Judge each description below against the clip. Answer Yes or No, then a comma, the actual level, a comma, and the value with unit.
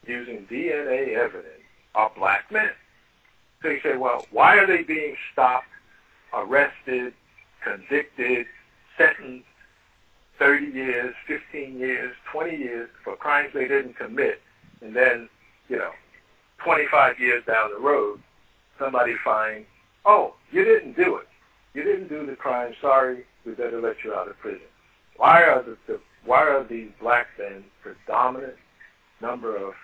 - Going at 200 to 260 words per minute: No, average, 140 wpm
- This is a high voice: No, medium, 140 Hz